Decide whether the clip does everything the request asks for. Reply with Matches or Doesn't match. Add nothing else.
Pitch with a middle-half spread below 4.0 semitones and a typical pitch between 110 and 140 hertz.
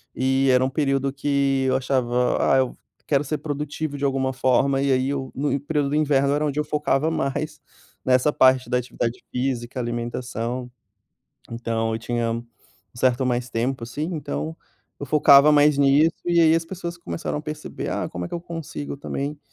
Matches